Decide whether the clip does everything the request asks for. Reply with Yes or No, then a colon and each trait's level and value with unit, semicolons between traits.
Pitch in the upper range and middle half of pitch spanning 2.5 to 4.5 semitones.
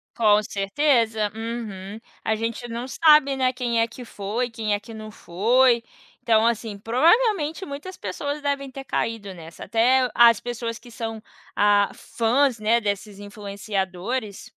Yes: high, 230 Hz; average, 3.7 semitones